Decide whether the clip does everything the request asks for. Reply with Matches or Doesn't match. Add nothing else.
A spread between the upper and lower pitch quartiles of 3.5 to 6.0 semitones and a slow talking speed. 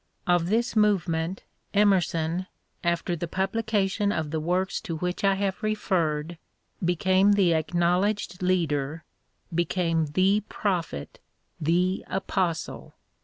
Doesn't match